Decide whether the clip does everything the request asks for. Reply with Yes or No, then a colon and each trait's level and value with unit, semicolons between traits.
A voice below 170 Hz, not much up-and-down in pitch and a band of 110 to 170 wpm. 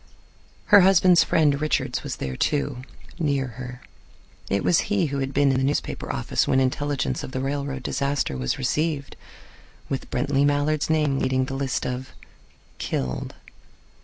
Yes: medium, 140 Hz; narrow, 2.0 semitones; average, 155 wpm